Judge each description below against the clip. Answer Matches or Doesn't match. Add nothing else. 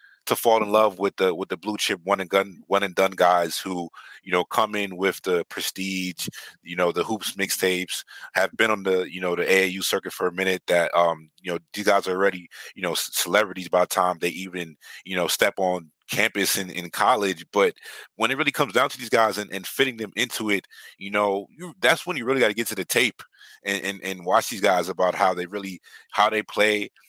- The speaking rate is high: Matches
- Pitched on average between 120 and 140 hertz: Doesn't match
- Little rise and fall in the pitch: Matches